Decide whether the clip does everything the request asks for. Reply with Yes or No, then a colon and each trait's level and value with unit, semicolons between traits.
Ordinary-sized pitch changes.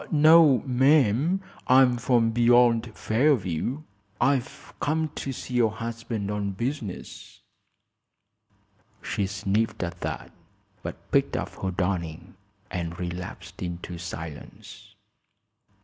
No: wide, 6.0 semitones